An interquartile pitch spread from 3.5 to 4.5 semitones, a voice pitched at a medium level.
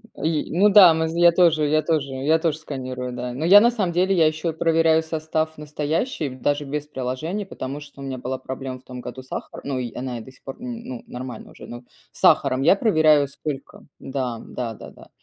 Yes: average, 3.9 semitones; medium, 150 Hz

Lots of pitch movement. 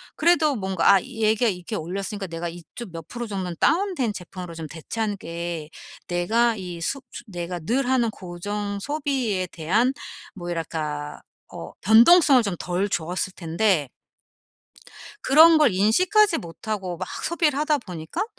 Yes: wide, 5.8 semitones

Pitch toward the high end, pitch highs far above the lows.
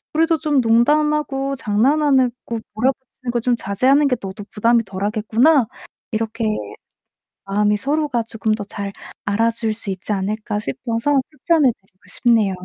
No: high, 230 Hz; average, 4.5 semitones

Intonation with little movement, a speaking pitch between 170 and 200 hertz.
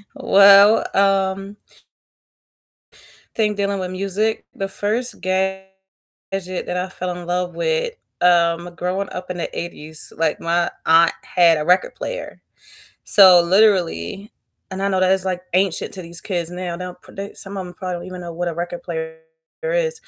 Yes: narrow, 2.2 semitones; medium, 185 Hz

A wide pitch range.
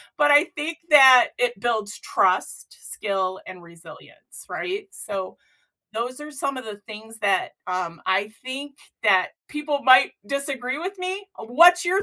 Yes: wide, 6.4 semitones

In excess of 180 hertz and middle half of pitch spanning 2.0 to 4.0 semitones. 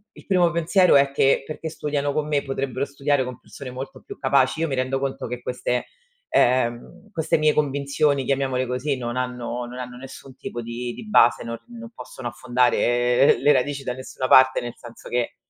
No: low, 130 Hz; average, 2.7 semitones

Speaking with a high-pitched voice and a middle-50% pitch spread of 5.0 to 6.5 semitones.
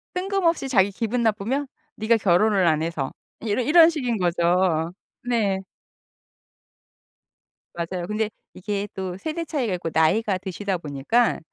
Yes: high, 205 Hz; average, 5.3 semitones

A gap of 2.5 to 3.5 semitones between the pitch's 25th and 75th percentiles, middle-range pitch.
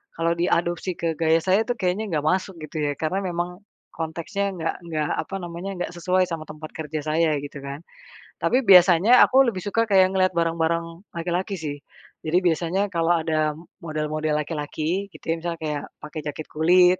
Yes: average, 2.9 semitones; medium, 170 Hz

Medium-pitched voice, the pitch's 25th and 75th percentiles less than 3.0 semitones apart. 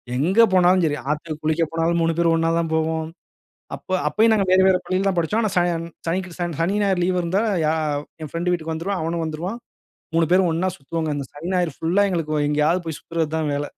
Yes: medium, 170 Hz; narrow, 2.4 semitones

